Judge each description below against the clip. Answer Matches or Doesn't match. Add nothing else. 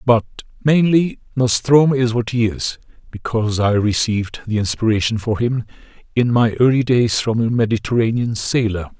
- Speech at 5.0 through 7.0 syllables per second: Matches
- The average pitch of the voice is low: Matches